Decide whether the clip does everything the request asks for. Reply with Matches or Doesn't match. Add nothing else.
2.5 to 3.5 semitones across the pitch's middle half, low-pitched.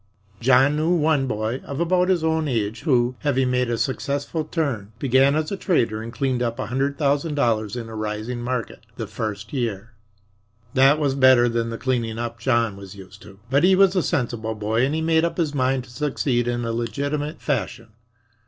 Doesn't match